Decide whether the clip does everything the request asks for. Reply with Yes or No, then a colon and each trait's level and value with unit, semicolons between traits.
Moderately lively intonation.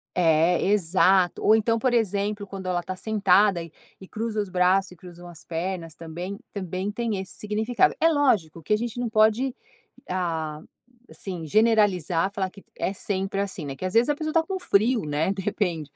Yes: average, 3.5 semitones